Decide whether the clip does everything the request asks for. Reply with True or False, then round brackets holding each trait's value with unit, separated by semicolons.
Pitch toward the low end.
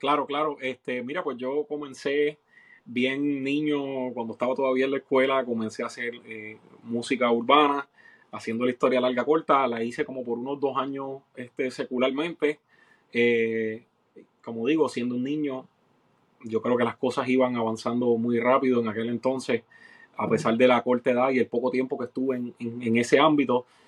True (125 Hz)